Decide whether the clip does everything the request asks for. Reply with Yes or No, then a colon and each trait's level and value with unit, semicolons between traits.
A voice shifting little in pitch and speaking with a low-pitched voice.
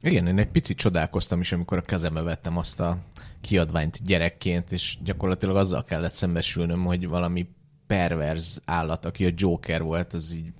Yes: narrow, 2.0 semitones; very low, 90 Hz